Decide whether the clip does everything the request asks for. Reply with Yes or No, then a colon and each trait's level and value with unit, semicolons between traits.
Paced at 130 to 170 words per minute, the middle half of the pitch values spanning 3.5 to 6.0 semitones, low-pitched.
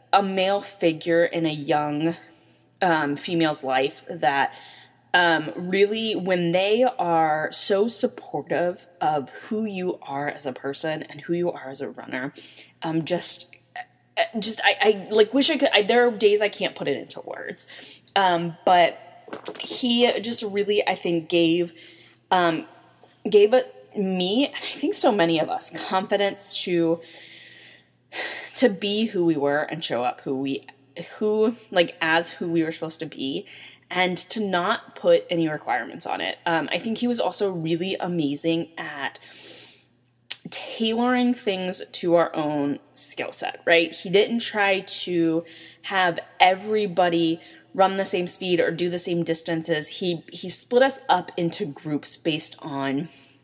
No: average, 155 wpm; average, 4.1 semitones; medium, 175 Hz